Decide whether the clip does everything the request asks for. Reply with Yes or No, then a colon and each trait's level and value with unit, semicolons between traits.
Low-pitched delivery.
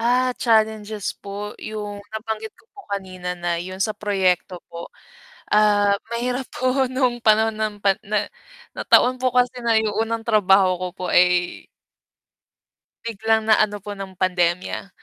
No: high, 210 Hz